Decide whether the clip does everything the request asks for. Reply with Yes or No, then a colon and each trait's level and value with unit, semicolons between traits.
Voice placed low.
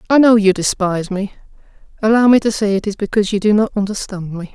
No: high, 205 Hz